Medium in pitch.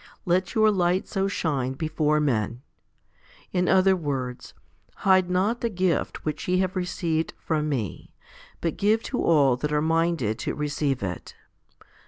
Yes: medium, 165 Hz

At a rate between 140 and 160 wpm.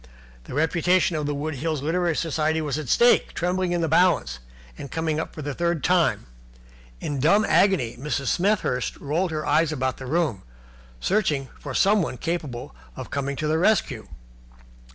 No: average, 170 wpm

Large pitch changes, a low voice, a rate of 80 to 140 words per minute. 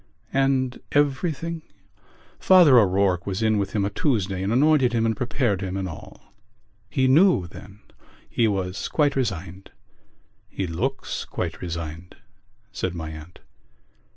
Yes: wide, 6.4 semitones; low, 105 Hz; slow, 135 wpm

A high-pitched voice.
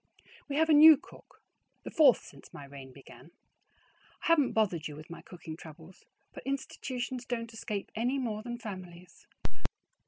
Yes: high, 220 Hz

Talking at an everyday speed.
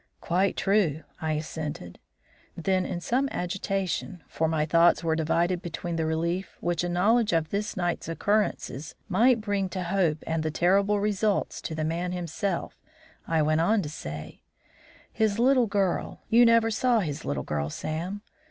Yes: average, 160 wpm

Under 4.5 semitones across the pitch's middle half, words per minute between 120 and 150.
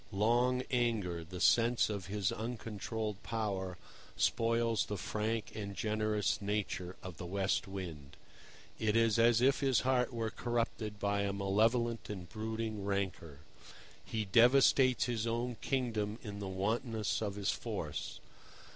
Yes: average, 2.8 semitones; average, 140 wpm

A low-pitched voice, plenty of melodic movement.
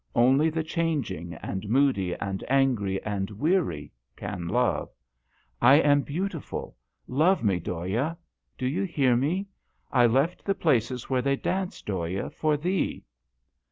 Yes: low, 130 Hz; wide, 7.9 semitones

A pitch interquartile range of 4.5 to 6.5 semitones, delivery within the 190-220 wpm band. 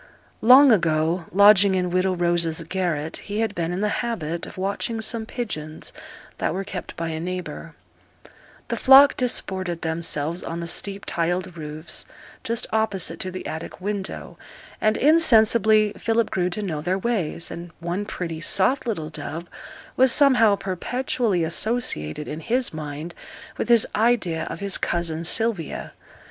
No: average, 4.8 semitones; average, 150 wpm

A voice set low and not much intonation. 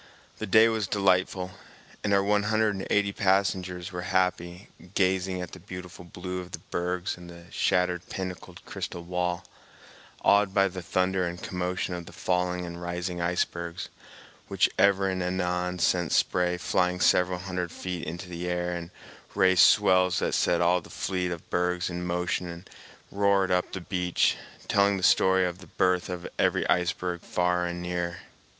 Yes: very low, 90 Hz; narrow, 1.1 semitones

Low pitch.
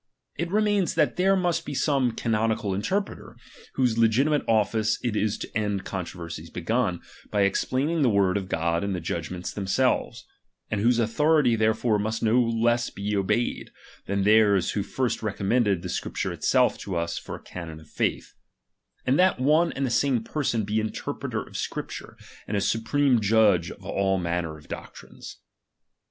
Yes: low, 110 Hz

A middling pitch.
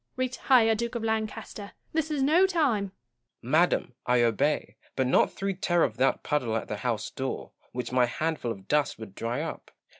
Yes: medium, 160 Hz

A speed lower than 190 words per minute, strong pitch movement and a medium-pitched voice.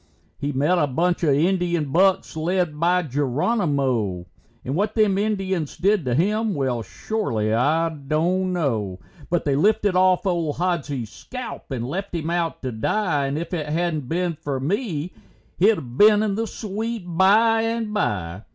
Yes: average, 160 wpm; wide, 5.7 semitones; medium, 170 Hz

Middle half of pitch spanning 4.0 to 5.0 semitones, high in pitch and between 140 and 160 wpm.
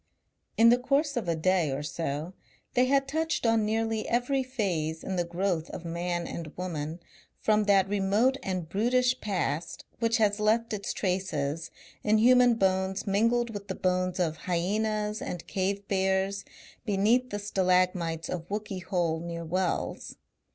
Yes: average, 4.3 semitones; high, 195 Hz; average, 155 wpm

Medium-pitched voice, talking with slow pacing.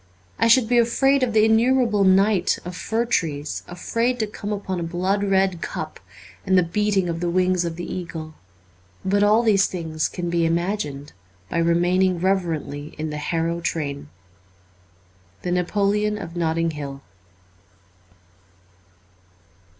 No: medium, 180 Hz; average, 145 wpm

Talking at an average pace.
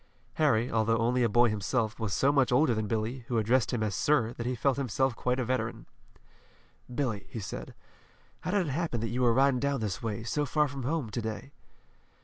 No: fast, 215 wpm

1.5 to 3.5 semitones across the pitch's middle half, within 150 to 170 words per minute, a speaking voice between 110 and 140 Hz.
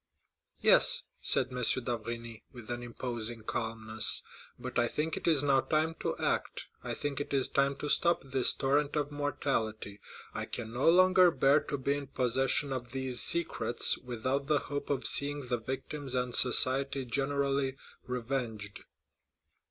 Yes: average, 2.9 semitones; average, 155 wpm; low, 135 Hz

